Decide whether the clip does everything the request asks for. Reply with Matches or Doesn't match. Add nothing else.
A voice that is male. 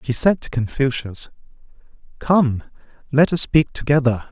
Matches